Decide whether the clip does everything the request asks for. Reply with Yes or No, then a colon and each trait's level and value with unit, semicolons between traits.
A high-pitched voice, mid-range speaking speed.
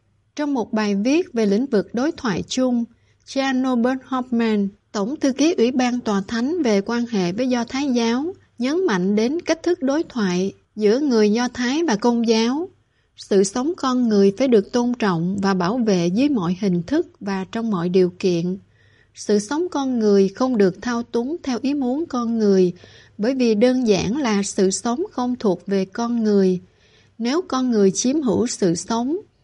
Yes: high, 235 Hz; average, 190 wpm